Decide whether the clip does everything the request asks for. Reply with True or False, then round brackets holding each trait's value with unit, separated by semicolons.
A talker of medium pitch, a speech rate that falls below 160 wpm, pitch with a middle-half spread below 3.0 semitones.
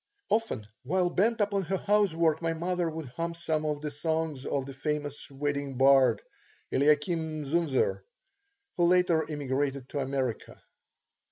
False (155 Hz; 140 wpm; 3.6 semitones)